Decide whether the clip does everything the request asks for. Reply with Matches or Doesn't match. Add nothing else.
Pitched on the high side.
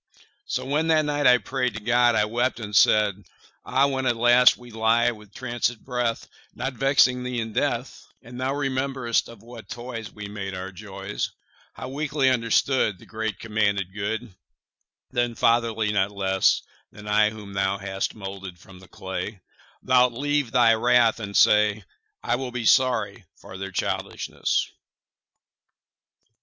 Doesn't match